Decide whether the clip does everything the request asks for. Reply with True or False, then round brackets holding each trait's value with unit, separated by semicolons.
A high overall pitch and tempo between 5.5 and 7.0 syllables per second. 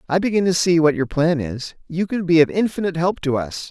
False (160 Hz; 5.9 syllables/s)